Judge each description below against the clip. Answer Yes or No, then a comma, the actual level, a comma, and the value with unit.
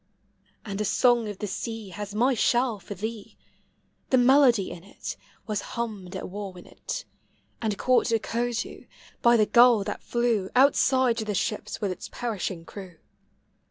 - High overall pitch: Yes, high, 220 Hz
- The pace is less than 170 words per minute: Yes, average, 160 wpm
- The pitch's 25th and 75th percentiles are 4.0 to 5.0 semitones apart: No, average, 3.1 semitones